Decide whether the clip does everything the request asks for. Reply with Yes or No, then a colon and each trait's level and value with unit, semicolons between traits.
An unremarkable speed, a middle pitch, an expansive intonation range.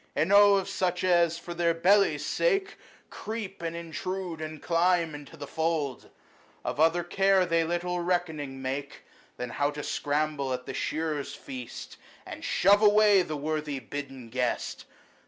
No: average, 150 wpm; medium, 165 Hz; average, 4.0 semitones